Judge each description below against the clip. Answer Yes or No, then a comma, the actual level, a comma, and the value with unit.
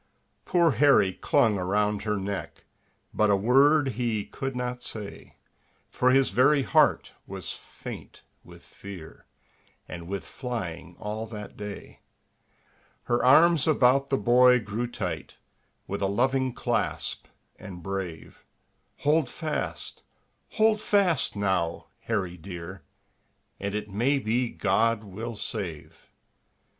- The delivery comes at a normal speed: No, slow, 120 wpm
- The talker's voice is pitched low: Yes, low, 110 Hz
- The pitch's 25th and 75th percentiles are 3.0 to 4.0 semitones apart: No, average, 4.9 semitones